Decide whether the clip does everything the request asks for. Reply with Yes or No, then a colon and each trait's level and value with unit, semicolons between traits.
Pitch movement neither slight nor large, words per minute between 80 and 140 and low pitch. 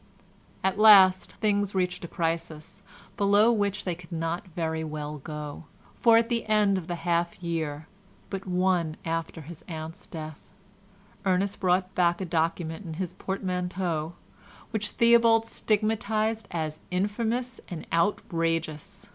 No: average, 3.8 semitones; slow, 135 wpm; medium, 180 Hz